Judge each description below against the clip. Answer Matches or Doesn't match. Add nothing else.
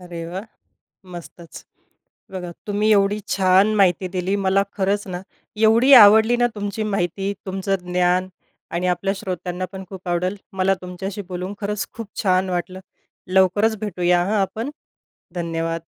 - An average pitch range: Doesn't match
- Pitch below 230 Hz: Matches